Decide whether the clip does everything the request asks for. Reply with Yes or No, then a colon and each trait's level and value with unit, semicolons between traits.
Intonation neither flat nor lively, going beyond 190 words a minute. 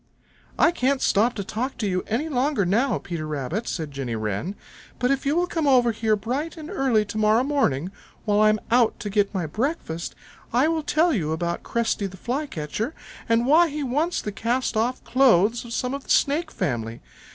No: wide, 6.2 semitones; average, 200 wpm